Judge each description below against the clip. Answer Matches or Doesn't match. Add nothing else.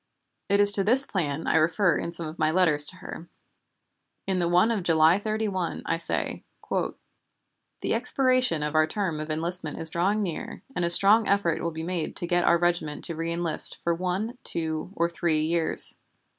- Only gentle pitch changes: Doesn't match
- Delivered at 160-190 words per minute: Matches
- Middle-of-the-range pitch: Matches